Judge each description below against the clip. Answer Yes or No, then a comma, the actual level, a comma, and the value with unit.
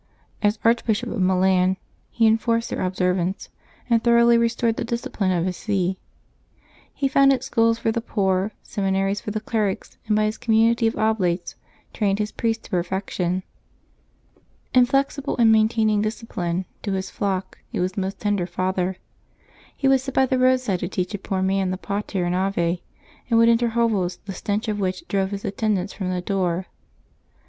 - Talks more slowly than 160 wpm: No, average, 170 wpm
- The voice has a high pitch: Yes, high, 205 Hz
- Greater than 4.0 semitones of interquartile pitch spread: No, average, 3.5 semitones